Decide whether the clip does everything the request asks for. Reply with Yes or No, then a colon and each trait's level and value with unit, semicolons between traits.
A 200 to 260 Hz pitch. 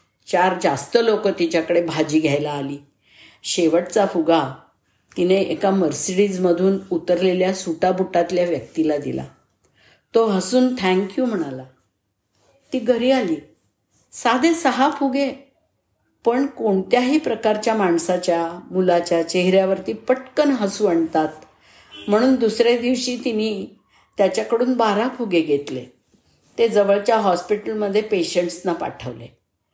No: medium, 185 Hz